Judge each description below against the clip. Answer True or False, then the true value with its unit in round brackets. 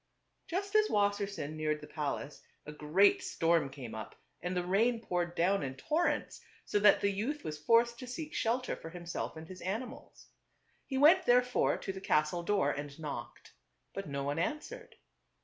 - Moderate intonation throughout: False (7.7 semitones)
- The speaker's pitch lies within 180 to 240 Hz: True (190 Hz)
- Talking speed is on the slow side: False (185 wpm)